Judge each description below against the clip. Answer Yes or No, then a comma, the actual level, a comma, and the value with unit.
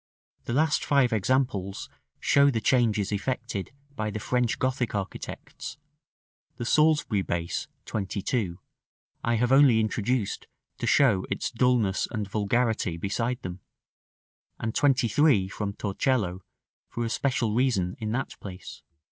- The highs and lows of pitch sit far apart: No, average, 4.3 semitones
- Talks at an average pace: No, slow, 125 wpm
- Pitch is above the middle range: No, low, 115 Hz